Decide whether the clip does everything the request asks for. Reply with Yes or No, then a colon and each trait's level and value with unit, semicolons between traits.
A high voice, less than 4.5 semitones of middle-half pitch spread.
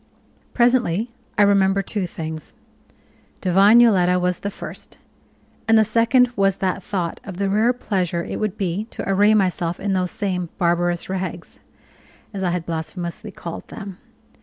Yes: high, 195 Hz; average, 3.1 semitones